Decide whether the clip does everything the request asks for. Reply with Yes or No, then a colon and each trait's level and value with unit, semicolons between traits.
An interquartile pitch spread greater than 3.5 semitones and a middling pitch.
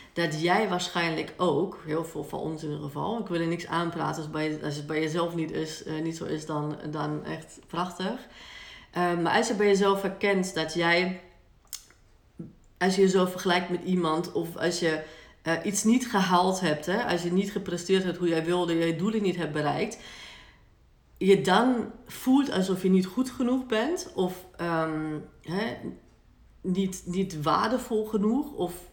No: average, 3.1 semitones; medium, 180 Hz